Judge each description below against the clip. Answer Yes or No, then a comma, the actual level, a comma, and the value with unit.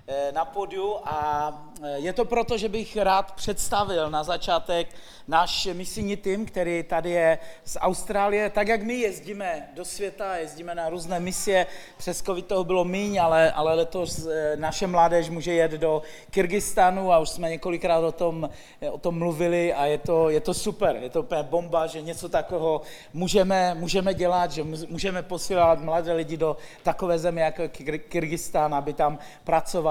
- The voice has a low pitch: No, medium, 170 Hz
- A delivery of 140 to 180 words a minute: Yes, average, 165 wpm